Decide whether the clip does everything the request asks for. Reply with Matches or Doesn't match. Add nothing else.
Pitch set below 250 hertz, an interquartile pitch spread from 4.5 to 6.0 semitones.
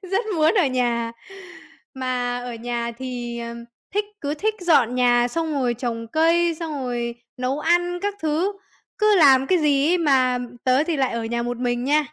Doesn't match